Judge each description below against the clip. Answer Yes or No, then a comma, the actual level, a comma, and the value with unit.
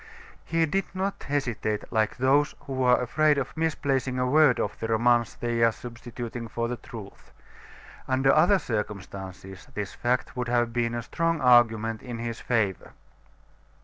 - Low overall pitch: Yes, low, 120 Hz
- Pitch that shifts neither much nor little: Yes, average, 3.0 semitones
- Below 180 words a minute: Yes, average, 155 wpm